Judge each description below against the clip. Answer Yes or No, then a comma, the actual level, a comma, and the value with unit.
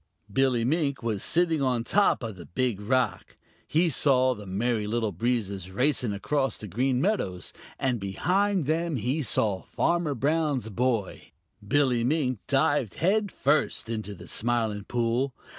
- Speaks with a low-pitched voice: Yes, low, 125 Hz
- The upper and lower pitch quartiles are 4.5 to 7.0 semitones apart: Yes, average, 5.1 semitones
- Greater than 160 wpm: No, average, 145 wpm